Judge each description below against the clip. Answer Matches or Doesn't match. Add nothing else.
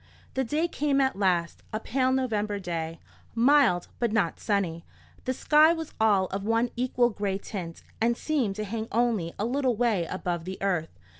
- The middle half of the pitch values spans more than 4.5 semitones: Matches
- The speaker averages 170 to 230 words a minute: Matches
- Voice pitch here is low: Doesn't match